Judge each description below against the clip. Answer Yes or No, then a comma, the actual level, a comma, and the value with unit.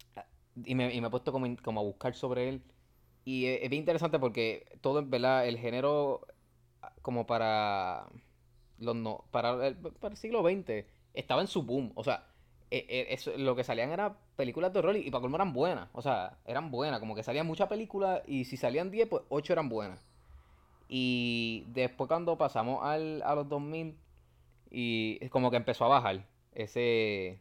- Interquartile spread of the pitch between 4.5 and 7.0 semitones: Yes, average, 5.1 semitones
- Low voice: Yes, low, 125 Hz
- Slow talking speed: No, fast, 190 wpm